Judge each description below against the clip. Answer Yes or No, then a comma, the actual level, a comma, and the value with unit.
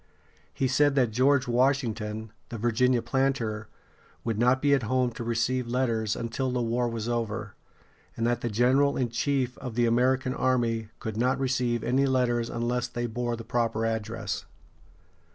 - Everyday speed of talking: Yes, average, 165 wpm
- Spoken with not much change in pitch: Yes, narrow, 2.0 semitones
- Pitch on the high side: No, low, 120 Hz